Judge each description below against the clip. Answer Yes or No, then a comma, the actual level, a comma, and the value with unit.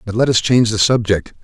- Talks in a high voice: No, low, 110 Hz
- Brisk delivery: Yes, fast, 250 wpm